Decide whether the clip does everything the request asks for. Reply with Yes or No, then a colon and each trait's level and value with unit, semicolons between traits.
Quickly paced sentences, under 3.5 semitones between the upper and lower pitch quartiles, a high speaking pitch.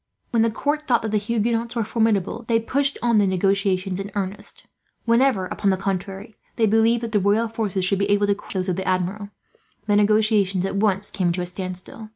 Yes: fast, 210 wpm; average, 2.9 semitones; high, 205 Hz